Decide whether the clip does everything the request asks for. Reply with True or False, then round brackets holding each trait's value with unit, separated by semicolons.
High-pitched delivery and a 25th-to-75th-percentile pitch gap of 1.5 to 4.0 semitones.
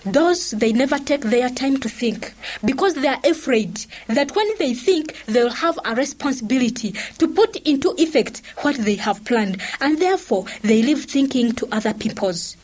False (255 Hz; 5.0 semitones)